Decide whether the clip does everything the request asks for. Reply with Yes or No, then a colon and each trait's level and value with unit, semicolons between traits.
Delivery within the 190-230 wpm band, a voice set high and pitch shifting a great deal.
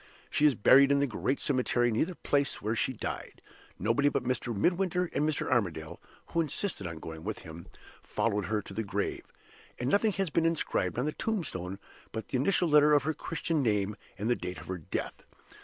No: fast, 205 wpm; low, 125 Hz; wide, 6.8 semitones